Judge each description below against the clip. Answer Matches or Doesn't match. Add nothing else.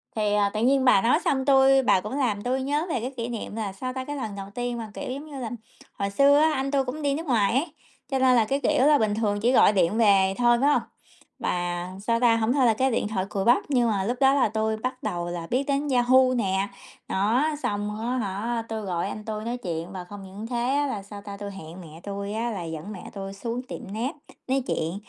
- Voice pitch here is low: Doesn't match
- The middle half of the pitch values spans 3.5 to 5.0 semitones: Matches